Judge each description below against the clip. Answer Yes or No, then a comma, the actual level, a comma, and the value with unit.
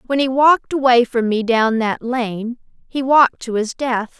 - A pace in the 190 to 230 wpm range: Yes, average, 200 wpm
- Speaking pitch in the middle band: No, high, 245 Hz